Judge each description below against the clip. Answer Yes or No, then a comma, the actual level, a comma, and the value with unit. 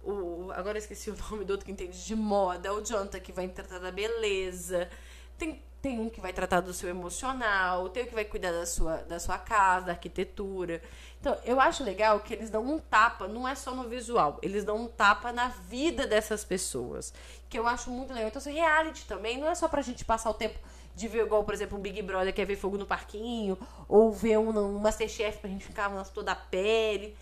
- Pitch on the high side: Yes, high, 210 Hz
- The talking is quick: Yes, fast, 230 wpm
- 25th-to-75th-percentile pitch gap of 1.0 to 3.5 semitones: Yes, average, 3.2 semitones